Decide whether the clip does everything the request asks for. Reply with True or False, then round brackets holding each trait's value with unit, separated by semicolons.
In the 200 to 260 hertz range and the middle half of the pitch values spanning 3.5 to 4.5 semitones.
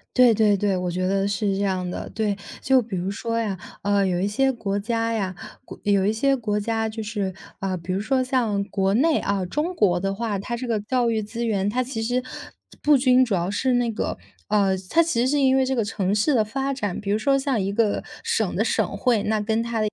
True (220 Hz; 3.9 semitones)